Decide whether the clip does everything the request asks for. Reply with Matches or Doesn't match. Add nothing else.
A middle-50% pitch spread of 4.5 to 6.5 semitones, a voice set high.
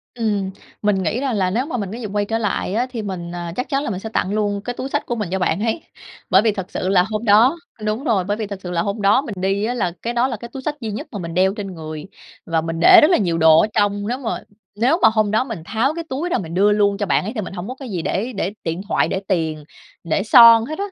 Doesn't match